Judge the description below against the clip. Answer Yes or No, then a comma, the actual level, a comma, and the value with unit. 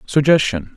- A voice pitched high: No, low, 130 Hz